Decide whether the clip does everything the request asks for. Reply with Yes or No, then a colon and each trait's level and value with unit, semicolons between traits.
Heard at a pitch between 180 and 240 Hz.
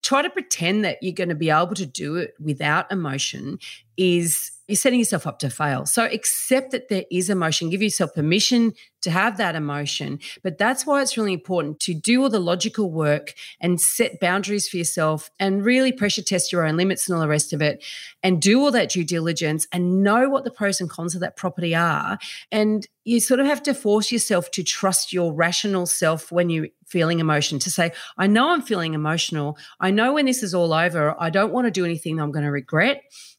Yes: medium, 185 Hz